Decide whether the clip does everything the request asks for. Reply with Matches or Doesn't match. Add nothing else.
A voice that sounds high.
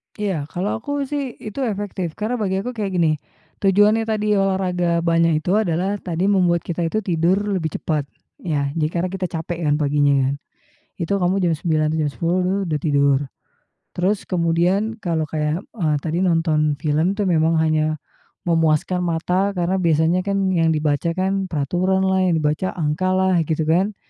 Doesn't match